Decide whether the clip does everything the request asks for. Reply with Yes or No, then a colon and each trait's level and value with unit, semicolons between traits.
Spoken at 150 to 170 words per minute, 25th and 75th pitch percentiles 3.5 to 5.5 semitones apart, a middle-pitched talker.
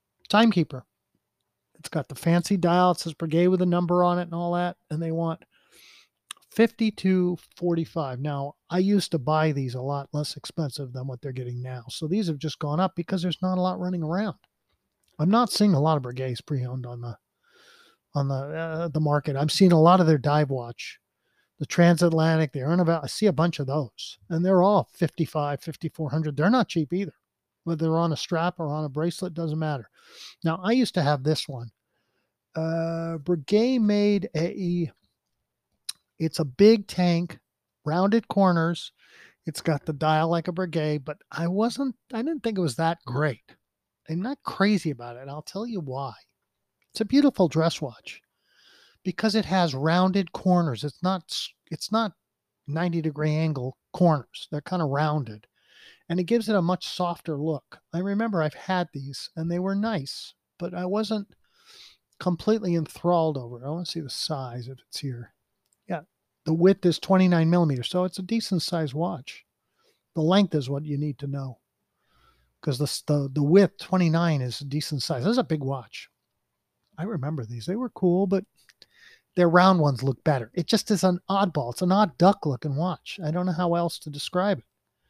No: average, 190 wpm; average, 3.9 semitones; medium, 165 Hz